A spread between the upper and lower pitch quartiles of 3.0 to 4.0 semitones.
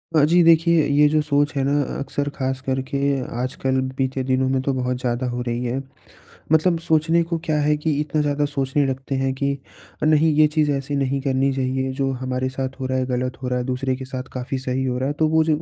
No: narrow, 2.4 semitones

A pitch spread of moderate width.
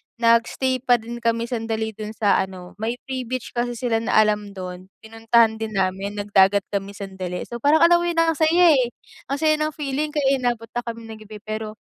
Yes: average, 3.7 semitones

